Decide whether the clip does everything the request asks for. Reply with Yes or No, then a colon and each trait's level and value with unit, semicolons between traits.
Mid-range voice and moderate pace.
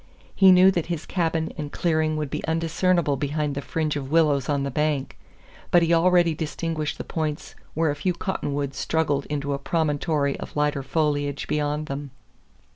Yes: medium, 150 Hz; average, 175 wpm